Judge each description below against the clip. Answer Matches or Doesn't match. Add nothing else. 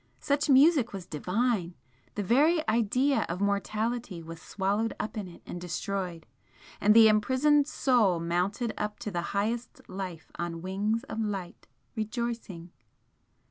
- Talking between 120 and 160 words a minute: Matches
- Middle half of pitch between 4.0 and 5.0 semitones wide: Matches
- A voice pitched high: Matches